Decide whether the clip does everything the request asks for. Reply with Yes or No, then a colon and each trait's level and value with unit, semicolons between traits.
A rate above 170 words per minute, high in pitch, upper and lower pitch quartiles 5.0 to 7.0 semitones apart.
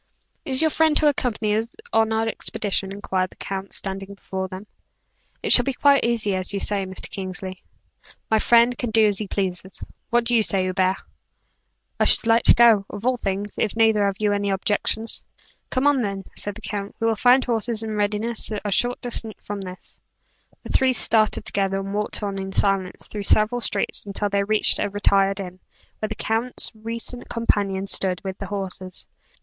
No: average, 195 wpm; high, 205 Hz; average, 2.7 semitones